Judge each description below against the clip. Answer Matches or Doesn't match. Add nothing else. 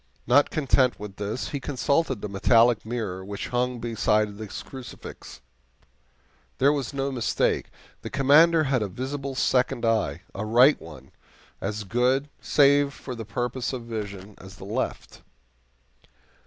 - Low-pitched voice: Matches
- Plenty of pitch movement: Doesn't match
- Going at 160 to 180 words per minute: Doesn't match